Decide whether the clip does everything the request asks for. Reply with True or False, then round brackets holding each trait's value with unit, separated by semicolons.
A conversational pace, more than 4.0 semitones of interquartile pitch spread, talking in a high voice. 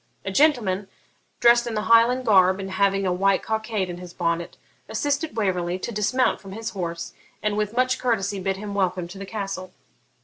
False (190 wpm; 3.4 semitones; 200 Hz)